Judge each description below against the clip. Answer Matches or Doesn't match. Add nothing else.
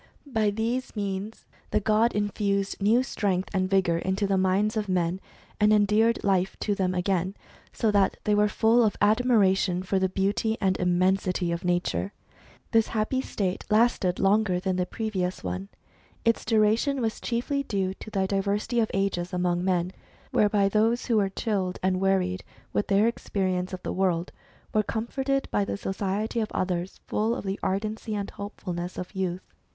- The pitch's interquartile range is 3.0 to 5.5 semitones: Doesn't match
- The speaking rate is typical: Matches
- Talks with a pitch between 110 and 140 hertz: Doesn't match